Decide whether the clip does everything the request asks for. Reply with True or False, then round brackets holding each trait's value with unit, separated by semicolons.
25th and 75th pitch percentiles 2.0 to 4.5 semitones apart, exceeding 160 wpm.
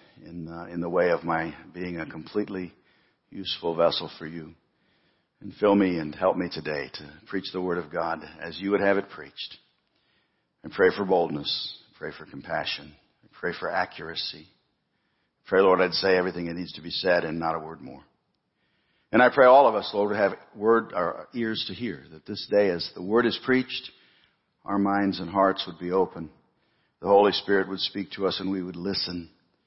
True (3.1 semitones; 200 wpm)